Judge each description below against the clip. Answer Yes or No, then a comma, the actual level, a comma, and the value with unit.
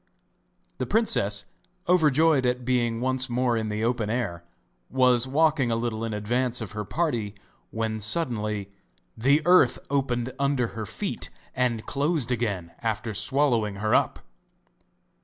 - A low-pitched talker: Yes, low, 120 Hz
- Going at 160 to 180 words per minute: No, average, 140 wpm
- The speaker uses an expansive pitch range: No, average, 3.4 semitones